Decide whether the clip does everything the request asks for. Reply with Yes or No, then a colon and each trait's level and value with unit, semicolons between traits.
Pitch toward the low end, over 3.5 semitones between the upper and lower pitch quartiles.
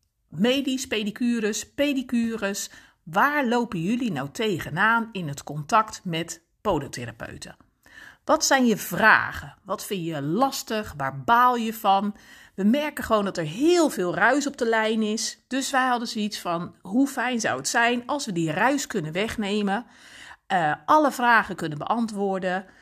No: high, 220 Hz; average, 4.3 semitones